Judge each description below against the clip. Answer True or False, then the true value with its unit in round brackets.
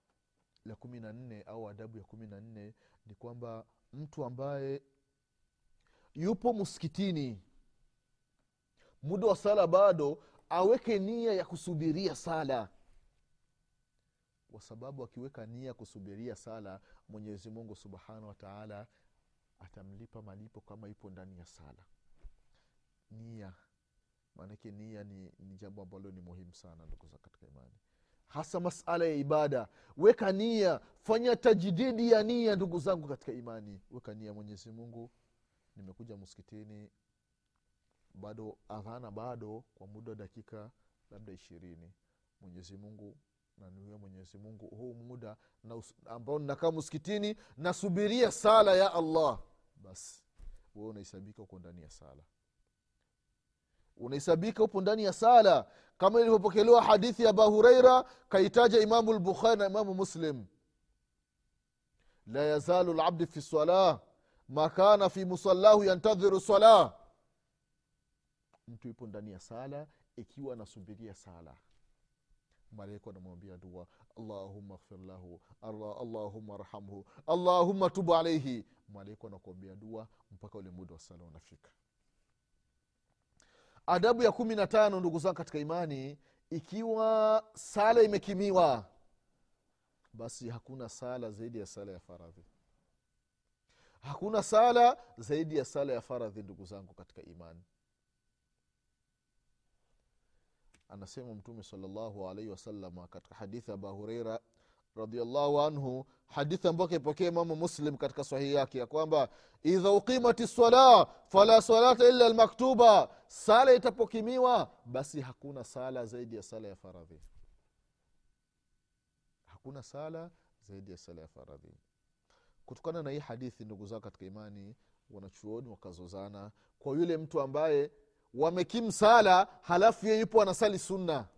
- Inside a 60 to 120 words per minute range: True (100 wpm)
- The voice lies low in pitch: True (120 Hz)